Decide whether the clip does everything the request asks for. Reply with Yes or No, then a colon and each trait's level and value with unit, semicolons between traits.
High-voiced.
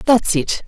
Yes: high, 200 Hz